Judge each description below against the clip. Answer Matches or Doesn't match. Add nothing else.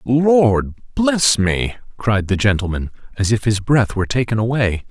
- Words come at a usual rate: Matches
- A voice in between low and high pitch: Doesn't match